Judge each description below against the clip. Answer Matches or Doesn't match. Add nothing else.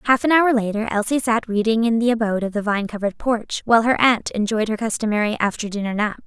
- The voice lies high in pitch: Matches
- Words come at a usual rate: Doesn't match